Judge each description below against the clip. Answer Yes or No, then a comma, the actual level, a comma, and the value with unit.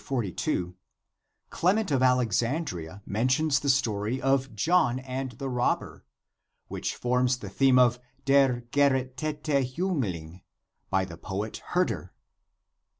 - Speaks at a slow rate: Yes, slow, 125 wpm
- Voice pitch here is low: Yes, low, 125 Hz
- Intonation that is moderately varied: Yes, average, 4.0 semitones